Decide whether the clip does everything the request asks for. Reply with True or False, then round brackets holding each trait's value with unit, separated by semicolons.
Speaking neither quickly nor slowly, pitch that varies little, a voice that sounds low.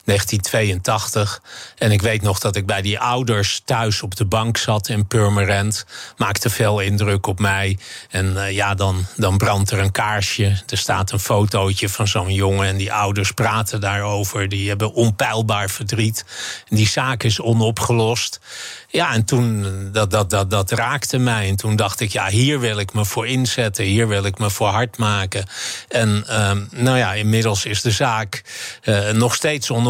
True (185 wpm; 2.2 semitones; 105 Hz)